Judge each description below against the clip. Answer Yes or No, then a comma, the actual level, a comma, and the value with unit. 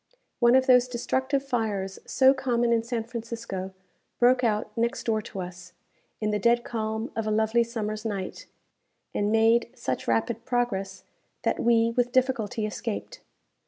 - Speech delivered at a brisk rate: No, average, 155 wpm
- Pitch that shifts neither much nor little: No, narrow, 2.3 semitones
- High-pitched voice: Yes, high, 230 Hz